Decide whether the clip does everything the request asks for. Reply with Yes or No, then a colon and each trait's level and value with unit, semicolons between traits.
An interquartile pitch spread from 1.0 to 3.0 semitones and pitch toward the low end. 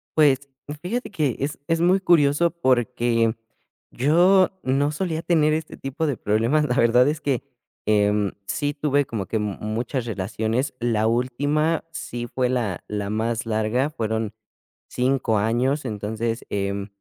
No: average, 5.1 semitones; low, 125 Hz